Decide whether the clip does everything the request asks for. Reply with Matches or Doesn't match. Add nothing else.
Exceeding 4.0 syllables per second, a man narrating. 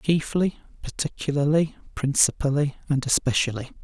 Matches